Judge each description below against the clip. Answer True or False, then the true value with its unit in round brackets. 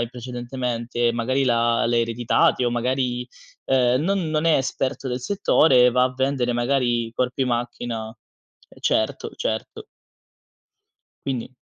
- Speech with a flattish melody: True (1.8 semitones)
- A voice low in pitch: True (125 Hz)